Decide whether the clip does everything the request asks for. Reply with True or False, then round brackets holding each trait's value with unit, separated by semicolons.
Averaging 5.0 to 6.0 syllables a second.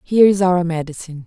False (6.8 syllables/s)